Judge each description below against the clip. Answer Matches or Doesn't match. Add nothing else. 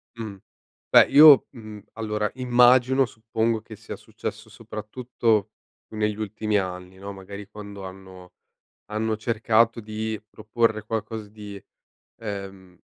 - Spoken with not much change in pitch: Matches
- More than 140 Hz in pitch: Doesn't match